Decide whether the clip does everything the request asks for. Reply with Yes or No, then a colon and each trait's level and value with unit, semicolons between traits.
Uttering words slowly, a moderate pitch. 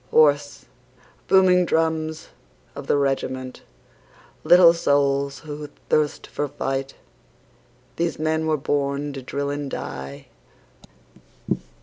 Yes: slow, 100 wpm; medium, 145 Hz